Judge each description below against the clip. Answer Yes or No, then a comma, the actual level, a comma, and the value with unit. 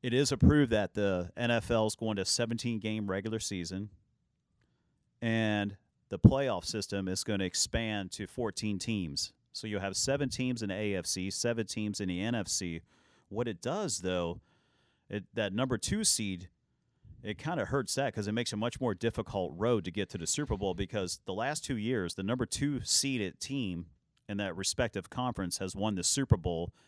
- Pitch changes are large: No, average, 3.7 semitones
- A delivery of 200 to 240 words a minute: No, average, 190 wpm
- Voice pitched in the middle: No, low, 105 Hz